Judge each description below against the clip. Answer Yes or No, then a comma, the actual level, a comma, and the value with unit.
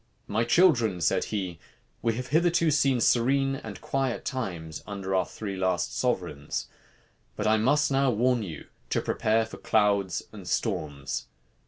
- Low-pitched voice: Yes, low, 110 Hz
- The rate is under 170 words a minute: Yes, average, 150 wpm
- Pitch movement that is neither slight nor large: No, wide, 5.8 semitones